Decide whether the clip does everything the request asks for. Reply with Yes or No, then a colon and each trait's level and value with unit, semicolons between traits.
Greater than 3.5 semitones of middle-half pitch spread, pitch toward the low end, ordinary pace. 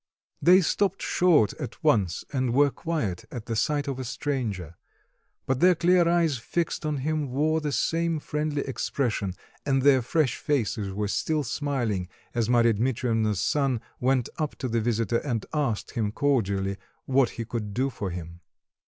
Yes: average, 5.2 semitones; low, 130 Hz; average, 165 wpm